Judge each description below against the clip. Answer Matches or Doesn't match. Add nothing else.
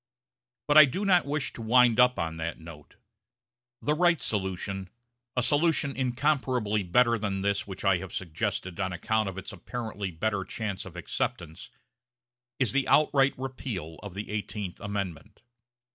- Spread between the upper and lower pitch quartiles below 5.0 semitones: Doesn't match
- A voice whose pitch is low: Matches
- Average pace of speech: Matches